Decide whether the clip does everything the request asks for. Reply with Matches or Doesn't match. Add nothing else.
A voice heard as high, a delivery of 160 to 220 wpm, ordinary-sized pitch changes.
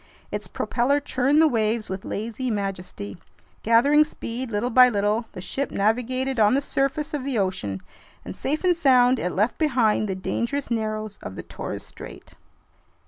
Matches